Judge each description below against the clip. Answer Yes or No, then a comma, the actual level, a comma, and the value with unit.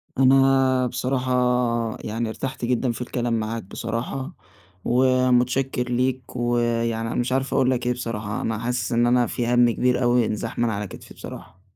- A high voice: No, low, 120 Hz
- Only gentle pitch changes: Yes, narrow, 1.7 semitones